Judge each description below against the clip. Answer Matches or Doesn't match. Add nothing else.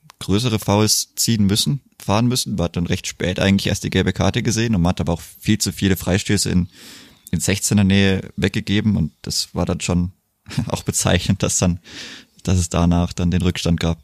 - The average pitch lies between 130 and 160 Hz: Doesn't match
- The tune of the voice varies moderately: Matches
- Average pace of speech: Doesn't match